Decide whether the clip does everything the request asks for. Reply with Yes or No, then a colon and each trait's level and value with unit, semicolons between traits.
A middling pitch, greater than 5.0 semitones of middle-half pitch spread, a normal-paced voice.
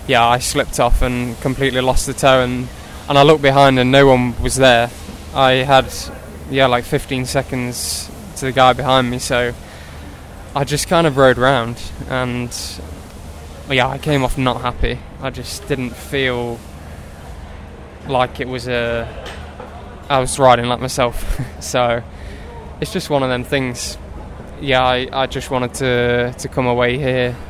No: low, 125 Hz; wide, 5.6 semitones; average, 160 wpm